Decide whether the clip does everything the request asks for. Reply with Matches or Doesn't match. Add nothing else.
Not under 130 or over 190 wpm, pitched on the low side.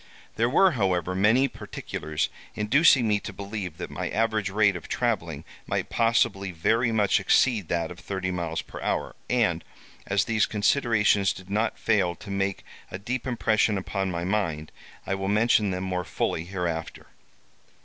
Matches